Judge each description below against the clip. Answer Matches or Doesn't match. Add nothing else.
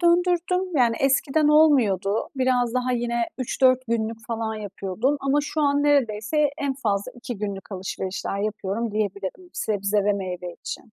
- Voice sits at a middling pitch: Doesn't match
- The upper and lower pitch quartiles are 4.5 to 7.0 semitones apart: Matches